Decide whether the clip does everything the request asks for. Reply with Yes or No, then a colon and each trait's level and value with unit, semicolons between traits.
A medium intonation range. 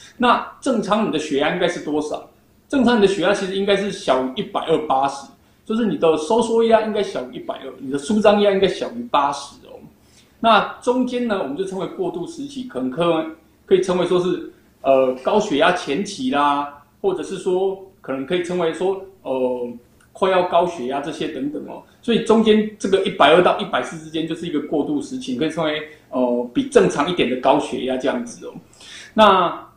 No: wide, 6.3 semitones